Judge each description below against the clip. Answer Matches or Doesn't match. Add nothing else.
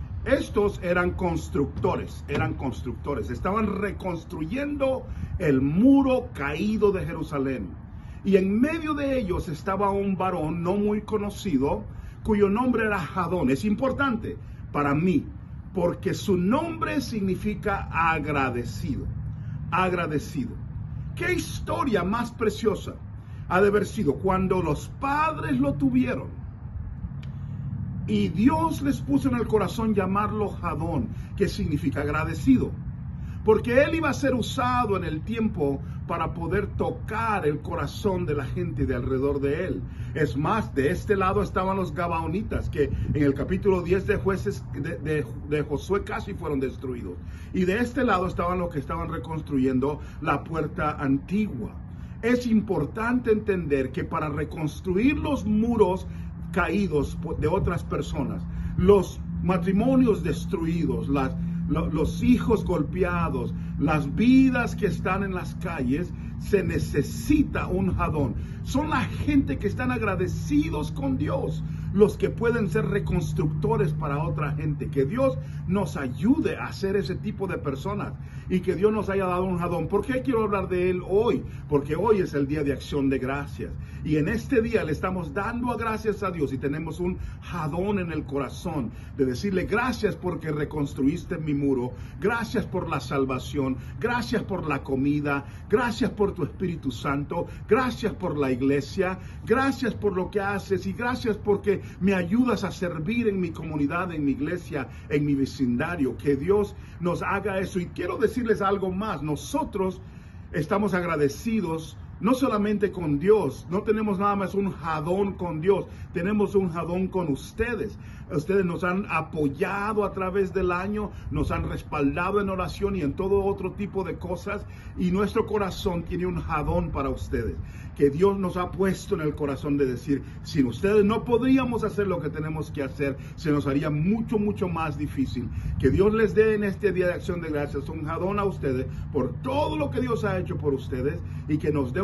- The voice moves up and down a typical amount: Doesn't match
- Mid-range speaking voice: Matches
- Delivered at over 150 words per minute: Matches